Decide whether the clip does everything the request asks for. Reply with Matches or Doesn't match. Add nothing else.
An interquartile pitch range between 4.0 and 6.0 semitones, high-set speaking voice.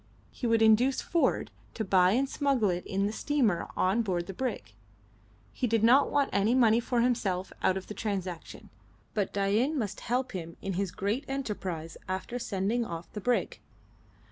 Matches